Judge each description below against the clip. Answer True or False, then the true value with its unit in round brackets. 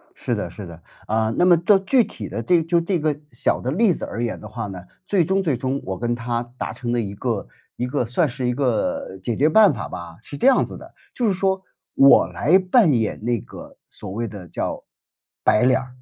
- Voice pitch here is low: True (130 Hz)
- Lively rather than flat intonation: True (7.8 semitones)